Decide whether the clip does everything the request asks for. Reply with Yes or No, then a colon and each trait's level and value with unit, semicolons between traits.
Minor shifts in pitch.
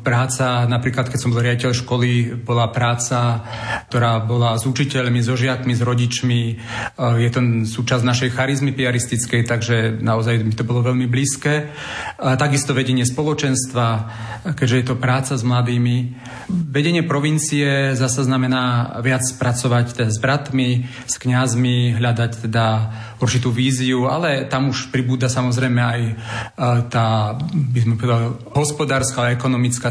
Yes: narrow, 1.6 semitones